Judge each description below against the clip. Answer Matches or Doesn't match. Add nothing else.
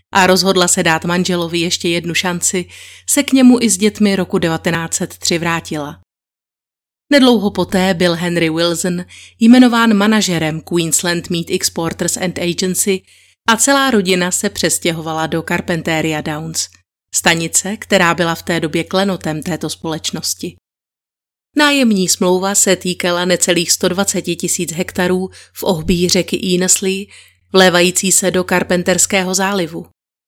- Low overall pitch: Doesn't match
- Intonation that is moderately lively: Doesn't match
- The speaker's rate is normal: Matches